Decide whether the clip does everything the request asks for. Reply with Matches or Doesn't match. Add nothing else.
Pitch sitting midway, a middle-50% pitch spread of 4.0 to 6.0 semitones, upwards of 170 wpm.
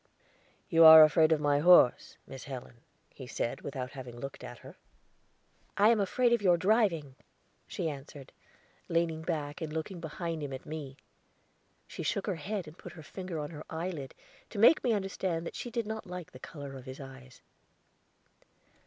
Matches